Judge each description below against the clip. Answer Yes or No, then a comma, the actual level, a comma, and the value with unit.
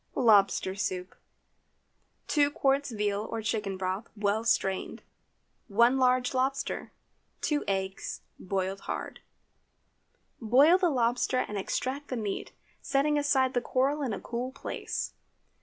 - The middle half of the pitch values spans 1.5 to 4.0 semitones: No, average, 5.0 semitones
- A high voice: Yes, high, 240 Hz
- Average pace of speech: No, slow, 120 wpm